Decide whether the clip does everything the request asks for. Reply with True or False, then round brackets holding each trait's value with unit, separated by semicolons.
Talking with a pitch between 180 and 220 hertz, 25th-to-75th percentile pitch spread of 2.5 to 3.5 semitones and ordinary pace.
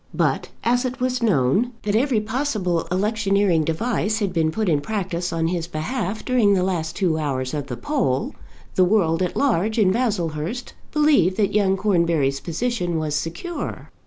False (190 Hz; 5.4 semitones; 165 wpm)